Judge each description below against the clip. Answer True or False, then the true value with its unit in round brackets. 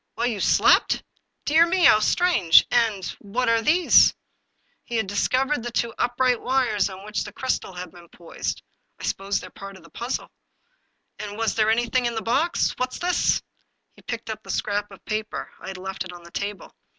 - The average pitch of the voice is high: True (225 Hz)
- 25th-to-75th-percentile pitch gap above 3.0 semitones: True (4.1 semitones)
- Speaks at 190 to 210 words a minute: True (200 wpm)